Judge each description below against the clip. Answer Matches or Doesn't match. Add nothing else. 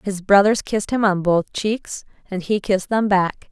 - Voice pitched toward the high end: Matches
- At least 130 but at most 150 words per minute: Doesn't match